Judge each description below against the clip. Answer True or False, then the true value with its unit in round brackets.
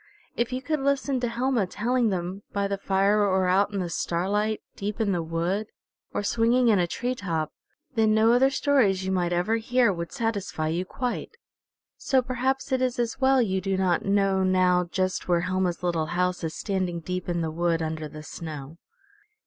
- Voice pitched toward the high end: True (195 Hz)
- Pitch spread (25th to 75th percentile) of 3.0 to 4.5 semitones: False (5.0 semitones)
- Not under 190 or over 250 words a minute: True (195 wpm)